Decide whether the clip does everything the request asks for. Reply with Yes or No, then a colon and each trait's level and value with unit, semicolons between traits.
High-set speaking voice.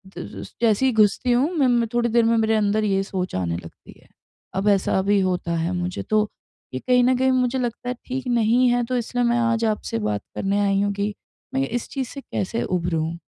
Yes: high, 220 Hz